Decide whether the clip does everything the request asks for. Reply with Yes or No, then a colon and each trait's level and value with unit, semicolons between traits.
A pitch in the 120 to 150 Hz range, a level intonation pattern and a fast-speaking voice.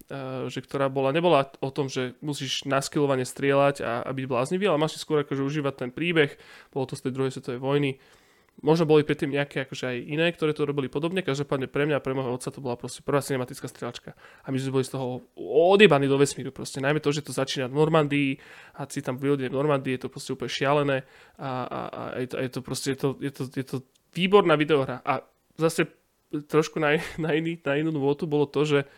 Yes: medium, 140 Hz; narrow, 2.2 semitones; fast, 205 wpm